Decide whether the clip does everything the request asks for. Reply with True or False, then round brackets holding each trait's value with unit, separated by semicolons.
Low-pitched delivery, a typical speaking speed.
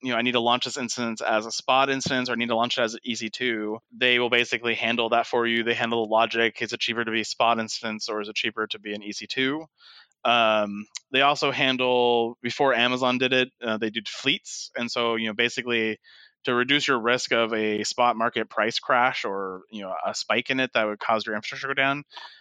False (115 Hz; 240 wpm)